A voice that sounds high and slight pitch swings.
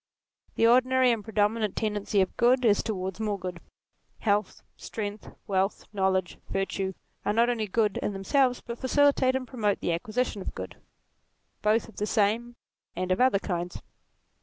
No: high, 210 Hz; average, 3.6 semitones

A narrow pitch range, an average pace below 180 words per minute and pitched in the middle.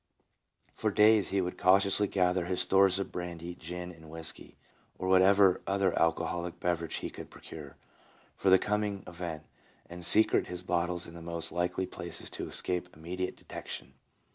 No: narrow, 2.0 semitones; average, 160 wpm; very low, 90 Hz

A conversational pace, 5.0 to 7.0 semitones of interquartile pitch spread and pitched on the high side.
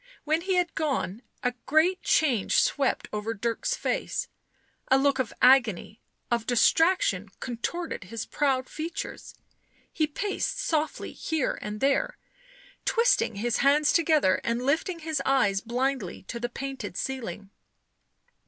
No: slow, 130 wpm; wide, 5.5 semitones; very high, 270 Hz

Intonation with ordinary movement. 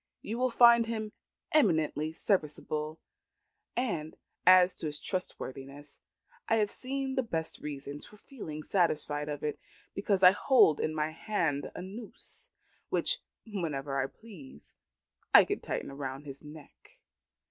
No: wide, 6.5 semitones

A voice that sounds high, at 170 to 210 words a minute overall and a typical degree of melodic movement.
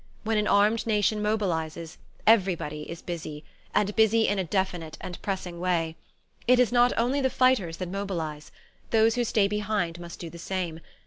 Yes: high, 195 Hz; average, 175 wpm; average, 4.4 semitones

